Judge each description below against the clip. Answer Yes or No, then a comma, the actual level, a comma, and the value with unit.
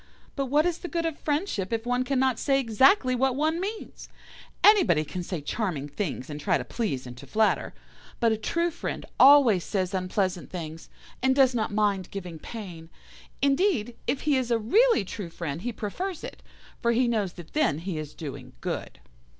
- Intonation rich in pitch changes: Yes, wide, 7.5 semitones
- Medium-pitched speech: No, high, 225 Hz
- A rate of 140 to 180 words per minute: No, average, 190 wpm